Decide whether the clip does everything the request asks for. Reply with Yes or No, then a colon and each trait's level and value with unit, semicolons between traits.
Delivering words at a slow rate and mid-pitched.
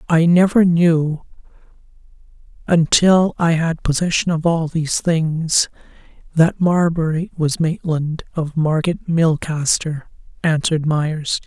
Yes: slow, 105 wpm; medium, 160 Hz